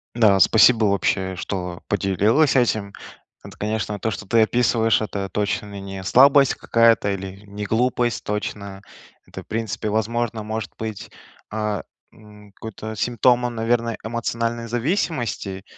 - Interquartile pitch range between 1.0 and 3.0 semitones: Yes, narrow, 2.6 semitones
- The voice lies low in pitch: Yes, low, 110 Hz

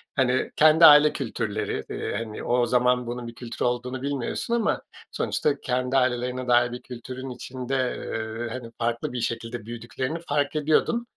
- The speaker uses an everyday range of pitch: No, narrow, 2.2 semitones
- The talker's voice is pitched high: No, low, 125 Hz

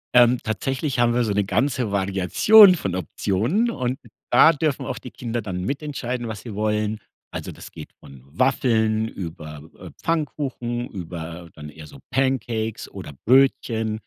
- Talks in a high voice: No, low, 115 Hz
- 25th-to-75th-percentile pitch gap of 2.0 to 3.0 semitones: No, average, 5.3 semitones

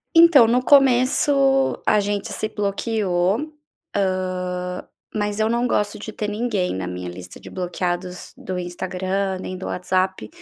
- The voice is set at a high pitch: Yes, high, 195 Hz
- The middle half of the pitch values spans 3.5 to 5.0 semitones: Yes, average, 3.8 semitones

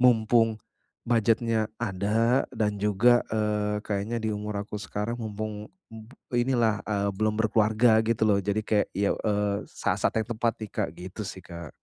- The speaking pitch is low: Yes, low, 110 Hz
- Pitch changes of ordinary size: No, narrow, 1.6 semitones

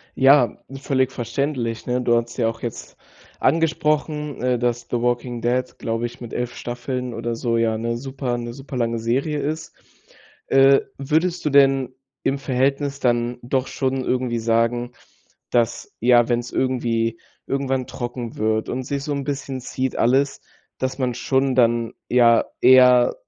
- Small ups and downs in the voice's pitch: Yes, narrow, 2.3 semitones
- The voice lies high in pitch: No, low, 125 Hz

